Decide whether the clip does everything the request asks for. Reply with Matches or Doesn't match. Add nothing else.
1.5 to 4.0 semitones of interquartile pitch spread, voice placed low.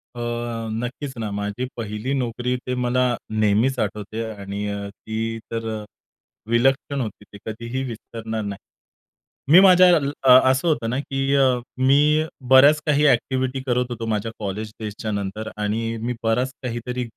Matches